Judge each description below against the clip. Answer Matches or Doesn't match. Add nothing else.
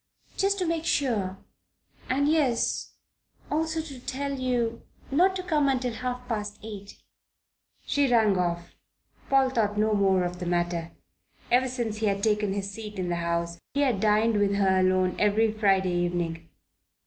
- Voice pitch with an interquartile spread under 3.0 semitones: Doesn't match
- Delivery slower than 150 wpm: Doesn't match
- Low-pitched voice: Doesn't match